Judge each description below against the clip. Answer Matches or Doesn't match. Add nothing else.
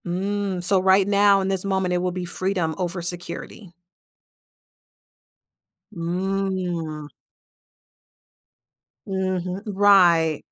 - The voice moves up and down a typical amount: Doesn't match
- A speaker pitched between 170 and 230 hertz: Matches